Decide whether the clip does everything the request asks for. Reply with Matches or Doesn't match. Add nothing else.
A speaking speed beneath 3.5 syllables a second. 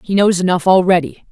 Doesn't match